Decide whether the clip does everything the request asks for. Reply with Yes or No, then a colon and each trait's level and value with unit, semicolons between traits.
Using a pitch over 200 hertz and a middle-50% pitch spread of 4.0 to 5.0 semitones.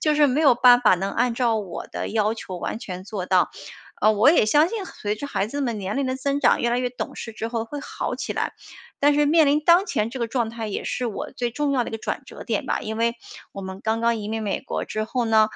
Yes: high, 235 Hz; average, 4.5 semitones